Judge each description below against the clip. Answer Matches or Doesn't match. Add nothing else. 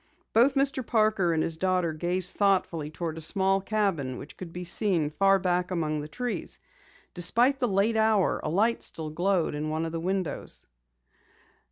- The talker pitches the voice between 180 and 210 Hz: Matches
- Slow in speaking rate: Doesn't match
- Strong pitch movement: Doesn't match